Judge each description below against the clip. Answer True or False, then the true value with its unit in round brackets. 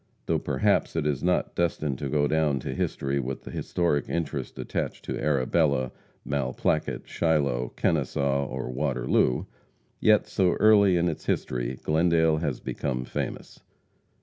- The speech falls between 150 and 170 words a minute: False (140 wpm)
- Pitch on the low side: True (75 Hz)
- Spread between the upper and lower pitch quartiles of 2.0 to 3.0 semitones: False (3.7 semitones)